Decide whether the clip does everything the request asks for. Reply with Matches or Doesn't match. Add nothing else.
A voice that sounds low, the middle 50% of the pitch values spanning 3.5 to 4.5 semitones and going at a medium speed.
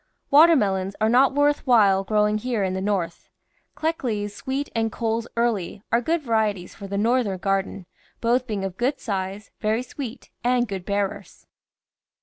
Doesn't match